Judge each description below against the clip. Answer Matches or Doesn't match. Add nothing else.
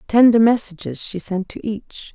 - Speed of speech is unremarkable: Matches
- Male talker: Doesn't match